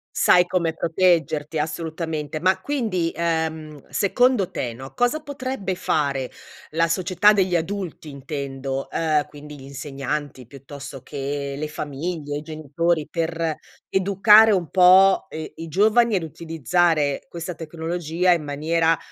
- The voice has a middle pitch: Yes, medium, 165 Hz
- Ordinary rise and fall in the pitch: Yes, average, 3.7 semitones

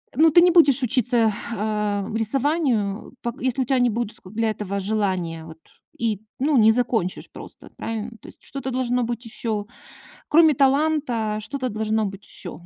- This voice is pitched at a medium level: No, high, 230 Hz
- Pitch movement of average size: Yes, average, 3.8 semitones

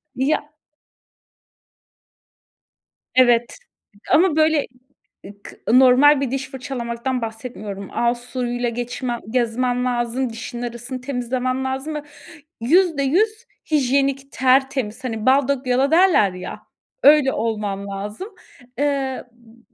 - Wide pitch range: No, average, 2.7 semitones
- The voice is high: Yes, very high, 255 Hz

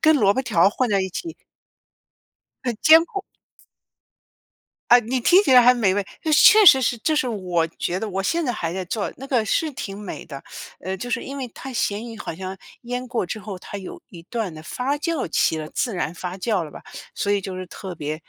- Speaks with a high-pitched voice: Yes, high, 215 Hz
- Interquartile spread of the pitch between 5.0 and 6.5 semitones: Yes, wide, 5.6 semitones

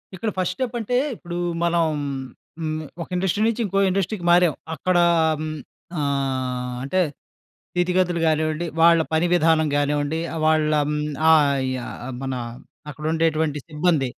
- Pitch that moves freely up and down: No, average, 3.1 semitones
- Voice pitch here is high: No, medium, 160 Hz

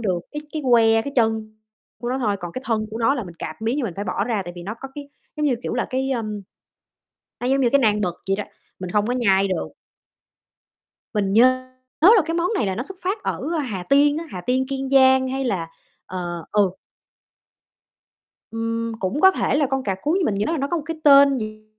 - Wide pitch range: No, average, 4.9 semitones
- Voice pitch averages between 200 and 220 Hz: No, high, 235 Hz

